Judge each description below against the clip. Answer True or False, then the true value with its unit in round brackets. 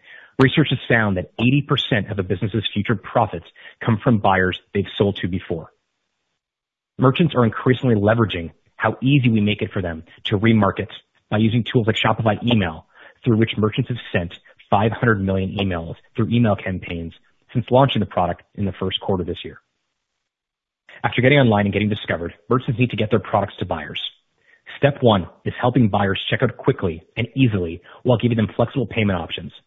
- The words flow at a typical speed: True (180 wpm)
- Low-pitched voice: True (110 Hz)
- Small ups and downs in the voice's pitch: False (3.7 semitones)